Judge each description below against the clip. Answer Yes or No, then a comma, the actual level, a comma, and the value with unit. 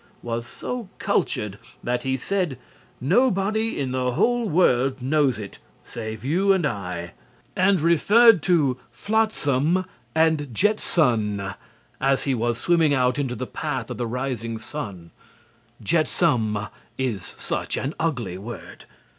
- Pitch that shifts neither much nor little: No, wide, 6.7 semitones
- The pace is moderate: No, slow, 130 wpm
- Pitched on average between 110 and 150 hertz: Yes, low, 135 Hz